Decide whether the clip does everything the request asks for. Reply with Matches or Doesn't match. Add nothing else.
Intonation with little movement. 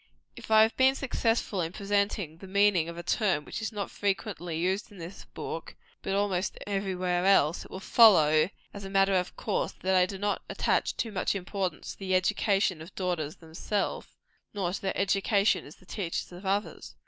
Matches